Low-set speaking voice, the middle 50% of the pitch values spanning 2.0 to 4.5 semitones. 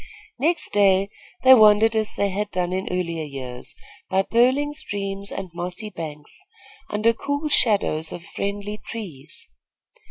No: high, 200 Hz; average, 3.9 semitones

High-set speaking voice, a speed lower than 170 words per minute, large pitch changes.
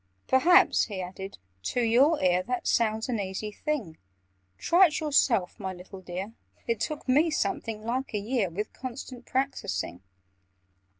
Yes: high, 230 Hz; average, 145 wpm; wide, 5.7 semitones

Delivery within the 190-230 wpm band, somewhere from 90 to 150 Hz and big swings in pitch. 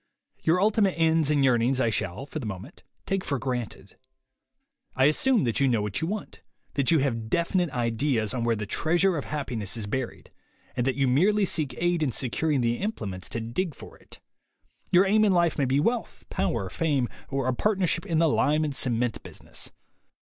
Yes: average, 195 wpm; medium, 140 Hz; wide, 6.1 semitones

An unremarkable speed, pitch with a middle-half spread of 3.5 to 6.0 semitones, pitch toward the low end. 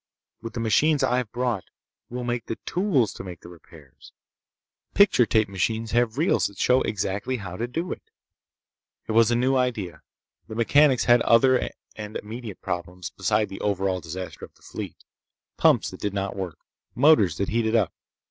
Yes: average, 175 wpm; average, 4.3 semitones; low, 110 Hz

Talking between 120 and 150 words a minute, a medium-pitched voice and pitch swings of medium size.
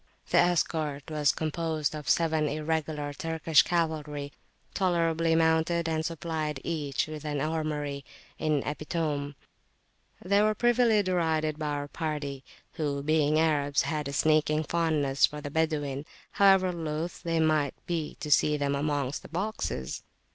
No: average, 140 wpm; medium, 155 Hz; narrow, 2.0 semitones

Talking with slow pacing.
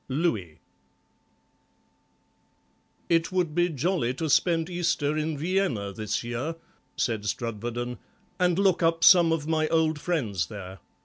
Yes: slow, 125 wpm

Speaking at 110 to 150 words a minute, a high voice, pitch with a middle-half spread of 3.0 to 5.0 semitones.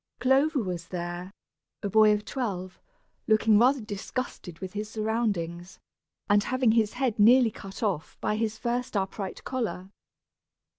Yes: average, 140 wpm; high, 215 Hz; average, 3.9 semitones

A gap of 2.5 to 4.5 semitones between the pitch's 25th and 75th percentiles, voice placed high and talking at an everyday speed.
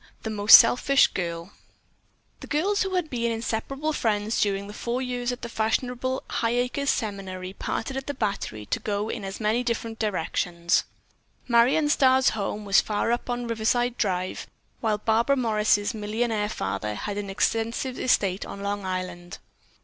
Yes: average, 3.5 semitones; high, 220 Hz; average, 155 wpm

